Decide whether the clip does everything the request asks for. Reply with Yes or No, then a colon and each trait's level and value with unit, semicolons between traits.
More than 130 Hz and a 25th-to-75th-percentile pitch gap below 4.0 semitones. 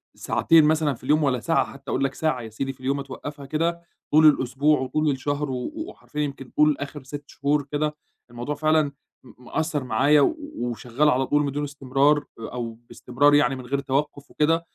Yes: medium, 140 Hz; narrow, 2.4 semitones